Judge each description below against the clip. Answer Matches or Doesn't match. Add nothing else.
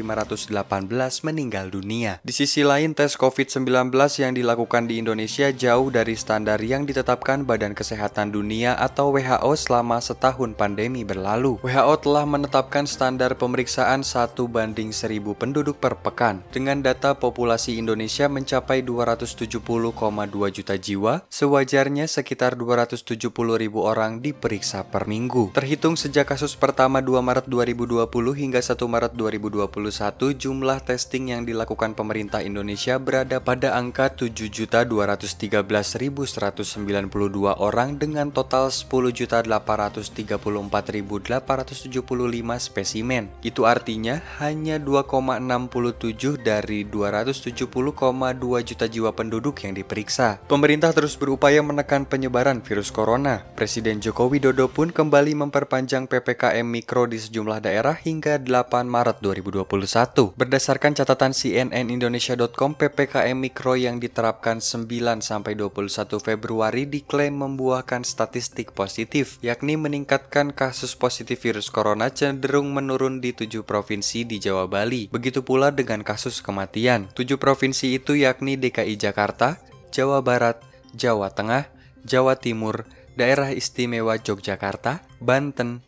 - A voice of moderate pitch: Doesn't match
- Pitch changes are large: Doesn't match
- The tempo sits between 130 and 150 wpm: Doesn't match